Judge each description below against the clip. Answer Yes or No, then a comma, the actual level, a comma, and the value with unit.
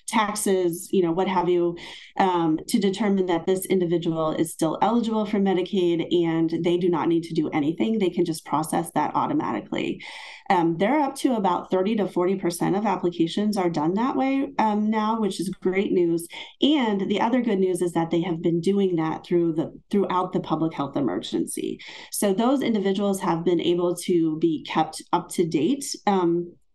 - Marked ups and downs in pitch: No, average, 3.6 semitones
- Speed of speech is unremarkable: Yes, average, 185 wpm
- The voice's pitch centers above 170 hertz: Yes, medium, 185 Hz